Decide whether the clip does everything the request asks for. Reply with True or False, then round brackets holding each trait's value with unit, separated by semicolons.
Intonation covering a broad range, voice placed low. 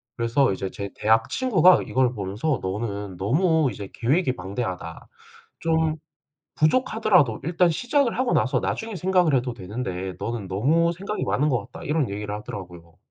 True (8.7 semitones; 125 Hz)